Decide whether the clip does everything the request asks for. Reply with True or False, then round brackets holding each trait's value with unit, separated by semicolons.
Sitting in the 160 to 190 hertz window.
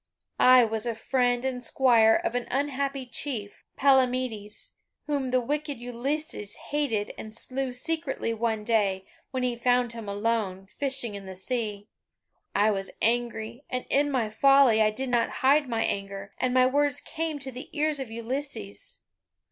False (245 Hz)